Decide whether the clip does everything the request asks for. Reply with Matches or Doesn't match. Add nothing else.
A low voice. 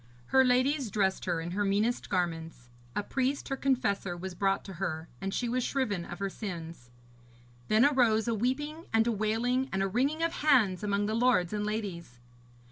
Doesn't match